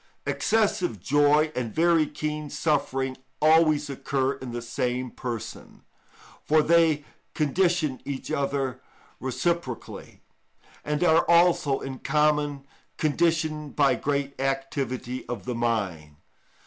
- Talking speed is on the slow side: Yes, slow, 110 wpm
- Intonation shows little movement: No, average, 3.1 semitones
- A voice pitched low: No, medium, 145 Hz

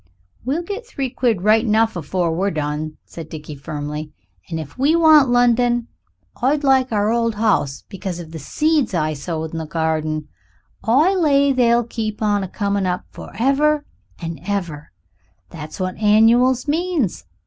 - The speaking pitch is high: Yes, high, 210 Hz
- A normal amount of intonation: No, wide, 8.0 semitones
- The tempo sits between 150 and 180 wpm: Yes, average, 160 wpm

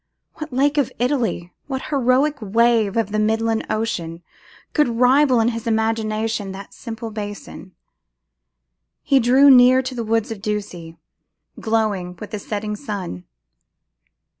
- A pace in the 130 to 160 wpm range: Yes, slow, 135 wpm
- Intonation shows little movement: No, average, 3.2 semitones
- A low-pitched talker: No, high, 225 Hz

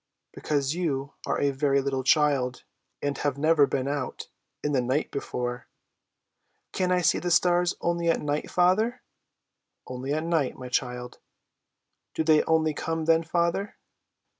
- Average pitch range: Yes, average, 3.8 semitones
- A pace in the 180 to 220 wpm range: No, average, 150 wpm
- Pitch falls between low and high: Yes, medium, 150 Hz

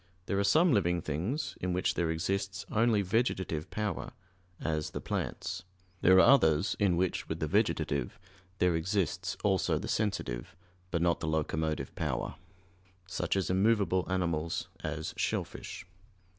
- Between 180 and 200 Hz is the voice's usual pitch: No, very low, 90 Hz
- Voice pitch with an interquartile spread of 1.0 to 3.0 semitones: No, average, 3.5 semitones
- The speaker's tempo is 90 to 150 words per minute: Yes, average, 145 wpm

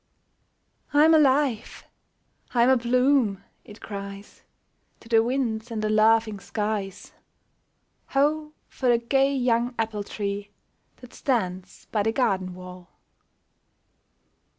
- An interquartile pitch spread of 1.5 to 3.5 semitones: No, average, 4.1 semitones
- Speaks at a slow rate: Yes, slow, 115 wpm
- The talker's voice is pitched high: Yes, high, 225 Hz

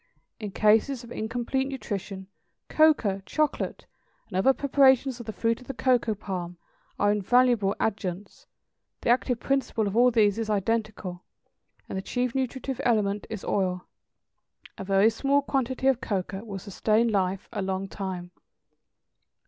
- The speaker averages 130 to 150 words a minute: Yes, average, 145 wpm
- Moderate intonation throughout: Yes, average, 4.4 semitones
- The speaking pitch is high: Yes, high, 220 Hz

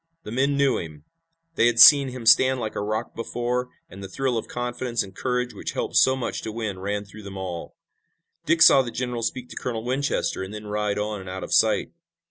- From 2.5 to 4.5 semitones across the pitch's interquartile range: Yes, average, 3.5 semitones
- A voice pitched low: Yes, low, 115 Hz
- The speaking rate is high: Yes, fast, 225 wpm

